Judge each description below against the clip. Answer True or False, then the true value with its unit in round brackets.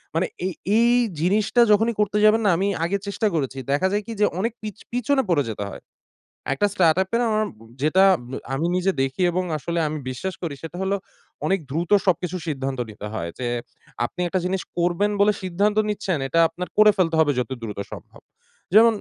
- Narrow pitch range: False (4.9 semitones)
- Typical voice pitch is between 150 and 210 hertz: True (185 Hz)